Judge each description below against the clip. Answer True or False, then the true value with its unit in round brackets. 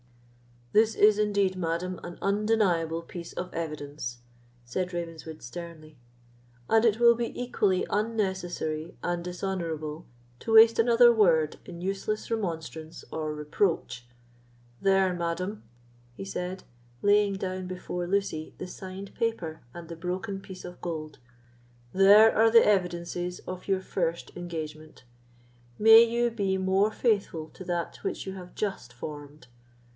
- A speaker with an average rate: False (130 wpm)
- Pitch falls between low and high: True (180 Hz)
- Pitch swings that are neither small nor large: True (3.9 semitones)